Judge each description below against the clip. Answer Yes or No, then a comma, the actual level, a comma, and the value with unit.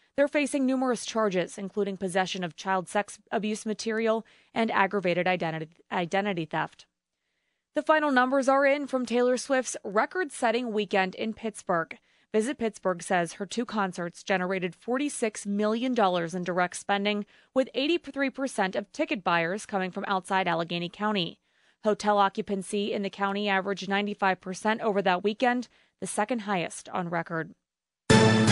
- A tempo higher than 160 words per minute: No, slow, 135 wpm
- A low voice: No, high, 205 Hz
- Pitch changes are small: No, average, 4.0 semitones